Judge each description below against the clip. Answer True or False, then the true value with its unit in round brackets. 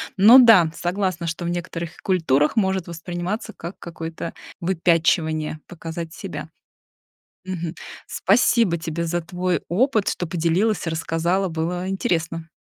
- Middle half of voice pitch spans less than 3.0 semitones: True (2.4 semitones)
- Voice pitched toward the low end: False (175 Hz)